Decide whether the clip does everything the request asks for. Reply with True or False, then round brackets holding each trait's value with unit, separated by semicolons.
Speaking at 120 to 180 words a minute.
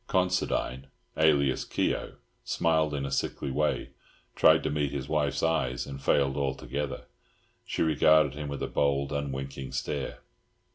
True (140 wpm)